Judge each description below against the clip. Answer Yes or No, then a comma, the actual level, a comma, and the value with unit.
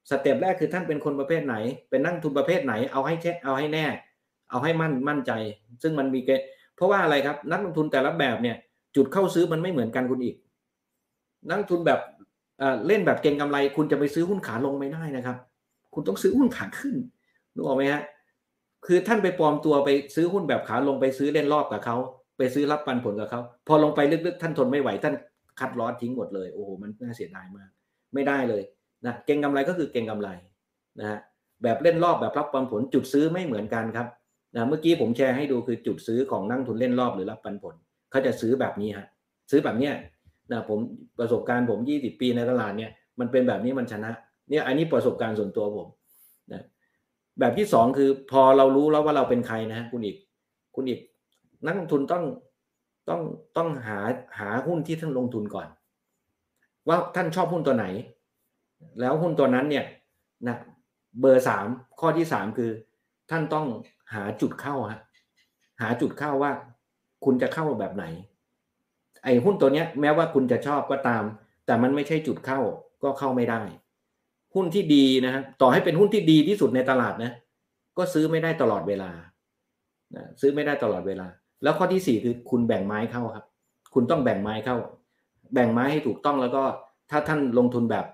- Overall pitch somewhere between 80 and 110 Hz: No, low, 135 Hz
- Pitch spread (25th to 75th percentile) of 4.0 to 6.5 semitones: Yes, average, 4.4 semitones